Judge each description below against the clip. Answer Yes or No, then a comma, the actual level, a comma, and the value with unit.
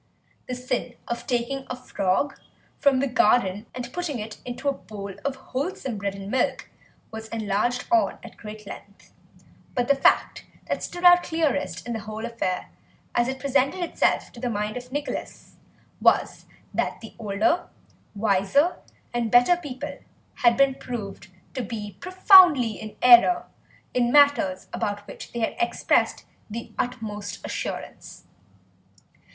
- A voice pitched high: Yes, high, 245 Hz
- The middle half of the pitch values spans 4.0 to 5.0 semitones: Yes, average, 4.4 semitones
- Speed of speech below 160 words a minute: Yes, average, 145 wpm